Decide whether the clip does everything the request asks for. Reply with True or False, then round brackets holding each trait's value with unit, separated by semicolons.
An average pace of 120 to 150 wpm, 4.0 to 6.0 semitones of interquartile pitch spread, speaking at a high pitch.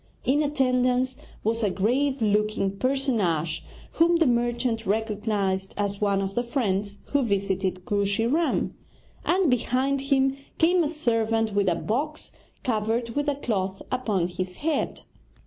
True (140 wpm; 5.1 semitones; 230 Hz)